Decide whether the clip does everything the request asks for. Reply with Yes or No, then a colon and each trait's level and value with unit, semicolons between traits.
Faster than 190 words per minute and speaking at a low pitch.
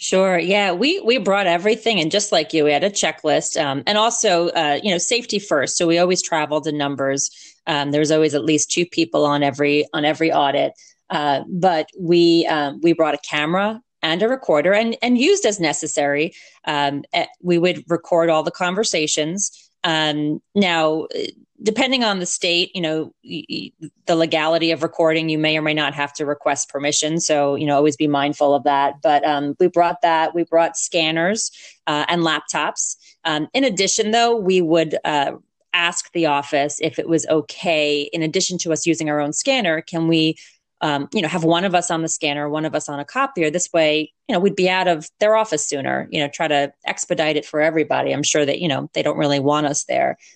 No: fast, 205 wpm; medium, 165 Hz